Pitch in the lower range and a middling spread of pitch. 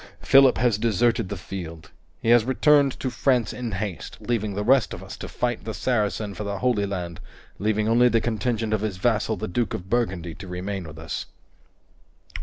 Yes: low, 110 Hz; average, 3.7 semitones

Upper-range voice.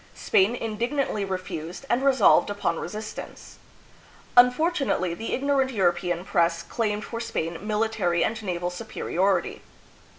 Yes: high, 210 Hz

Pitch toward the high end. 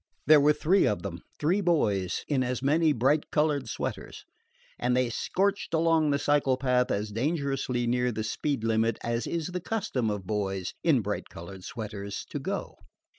No: low, 125 Hz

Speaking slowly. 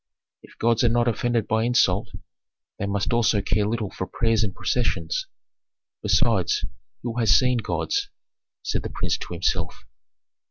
No: average, 150 wpm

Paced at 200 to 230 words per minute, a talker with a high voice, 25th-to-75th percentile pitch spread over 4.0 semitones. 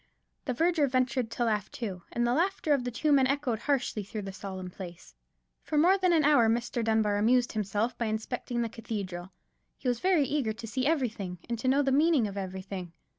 Yes: fast, 205 wpm; high, 240 Hz; average, 5.0 semitones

